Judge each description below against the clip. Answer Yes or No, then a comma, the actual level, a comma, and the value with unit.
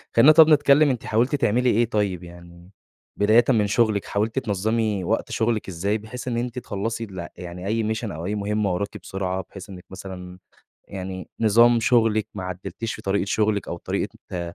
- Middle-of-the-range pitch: No, low, 105 Hz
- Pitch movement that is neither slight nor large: Yes, average, 3.5 semitones